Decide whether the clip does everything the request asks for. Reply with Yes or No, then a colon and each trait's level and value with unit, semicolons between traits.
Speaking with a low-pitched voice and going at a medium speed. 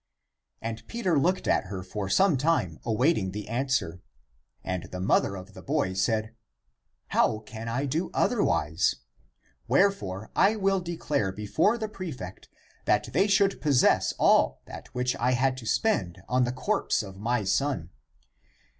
Yes: low, 125 Hz; average, 155 wpm